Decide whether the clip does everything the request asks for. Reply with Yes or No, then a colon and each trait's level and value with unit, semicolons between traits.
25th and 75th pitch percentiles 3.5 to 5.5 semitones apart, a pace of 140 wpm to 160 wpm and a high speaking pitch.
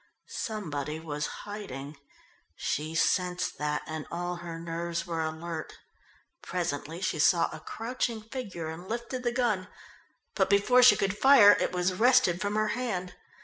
No: average, 4.8 semitones; average, 145 wpm; medium, 180 Hz